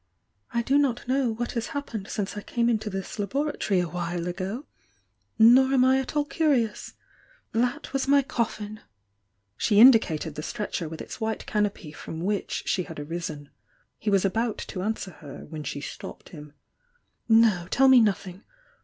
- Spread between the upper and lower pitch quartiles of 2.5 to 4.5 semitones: No, wide, 5.4 semitones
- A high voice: Yes, high, 215 Hz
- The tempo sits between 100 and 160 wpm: No, average, 175 wpm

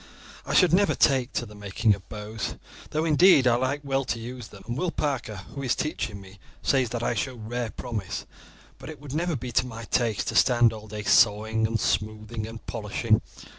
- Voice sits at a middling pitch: No, low, 115 Hz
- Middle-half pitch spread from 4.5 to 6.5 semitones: No, average, 3.8 semitones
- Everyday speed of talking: No, fast, 210 wpm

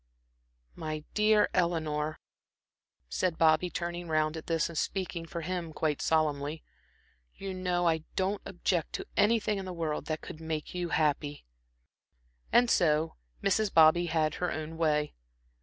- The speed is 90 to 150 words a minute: Yes, average, 145 wpm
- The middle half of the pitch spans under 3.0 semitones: Yes, narrow, 2.5 semitones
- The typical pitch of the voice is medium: Yes, medium, 165 Hz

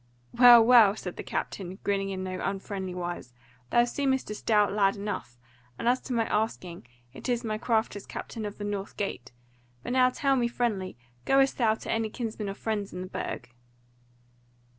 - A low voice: No, high, 210 Hz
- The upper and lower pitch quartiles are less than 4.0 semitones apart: Yes, average, 3.5 semitones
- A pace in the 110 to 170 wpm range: No, average, 185 wpm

